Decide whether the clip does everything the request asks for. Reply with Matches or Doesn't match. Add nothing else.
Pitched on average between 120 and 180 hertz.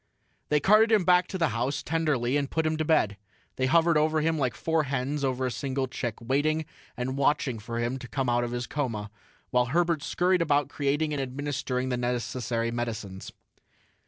Matches